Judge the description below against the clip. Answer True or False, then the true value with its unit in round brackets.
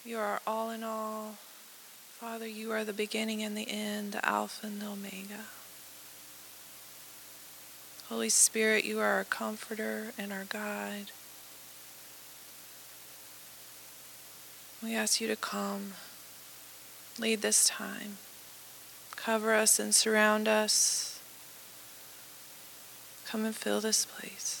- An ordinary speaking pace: False (110 wpm)